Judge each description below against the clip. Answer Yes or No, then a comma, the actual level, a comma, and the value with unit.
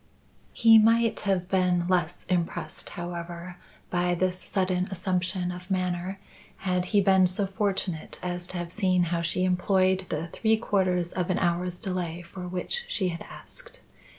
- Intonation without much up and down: Yes, narrow, 1.4 semitones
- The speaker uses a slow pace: No, average, 155 wpm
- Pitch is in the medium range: Yes, medium, 180 Hz